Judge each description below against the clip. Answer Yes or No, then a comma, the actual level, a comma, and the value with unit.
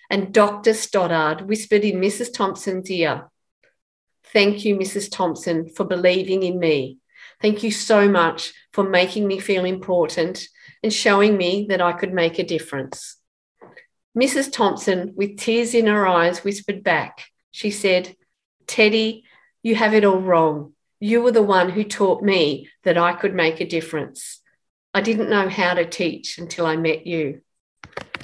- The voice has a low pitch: No, high, 195 Hz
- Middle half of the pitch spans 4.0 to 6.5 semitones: No, average, 3.4 semitones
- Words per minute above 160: No, average, 155 wpm